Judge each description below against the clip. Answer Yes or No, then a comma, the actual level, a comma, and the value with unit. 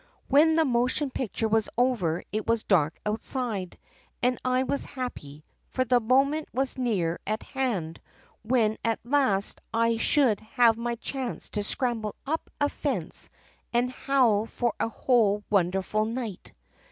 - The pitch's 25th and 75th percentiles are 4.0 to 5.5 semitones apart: No, average, 3.5 semitones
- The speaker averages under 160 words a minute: Yes, average, 145 wpm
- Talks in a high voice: Yes, high, 235 Hz